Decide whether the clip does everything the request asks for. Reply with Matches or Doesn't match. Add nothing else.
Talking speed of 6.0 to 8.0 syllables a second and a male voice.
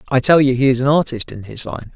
Matches